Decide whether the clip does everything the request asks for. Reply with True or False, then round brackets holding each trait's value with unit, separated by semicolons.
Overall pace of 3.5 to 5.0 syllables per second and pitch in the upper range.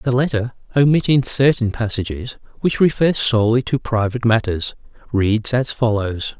False (4.9 syllables/s; 120 Hz)